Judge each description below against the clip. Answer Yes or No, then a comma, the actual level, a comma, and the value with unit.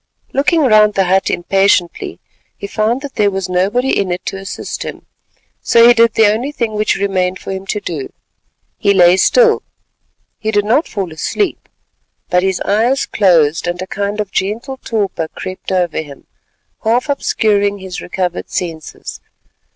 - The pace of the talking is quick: No, average, 160 wpm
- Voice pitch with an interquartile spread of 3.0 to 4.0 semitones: Yes, average, 3.5 semitones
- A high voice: Yes, high, 200 Hz